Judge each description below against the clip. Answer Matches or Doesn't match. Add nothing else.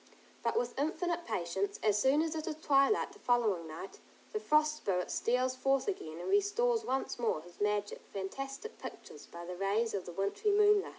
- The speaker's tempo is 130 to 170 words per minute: Doesn't match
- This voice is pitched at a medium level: Doesn't match